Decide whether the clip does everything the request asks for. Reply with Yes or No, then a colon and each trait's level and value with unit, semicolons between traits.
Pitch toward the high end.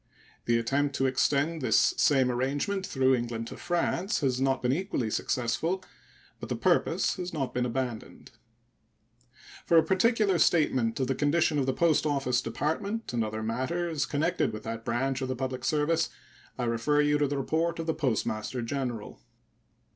No: low, 135 Hz